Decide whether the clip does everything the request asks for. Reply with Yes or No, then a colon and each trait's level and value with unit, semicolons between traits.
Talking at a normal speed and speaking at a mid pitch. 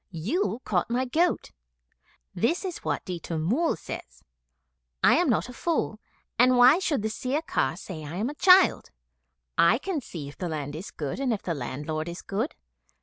No: average, 180 wpm; high, 215 Hz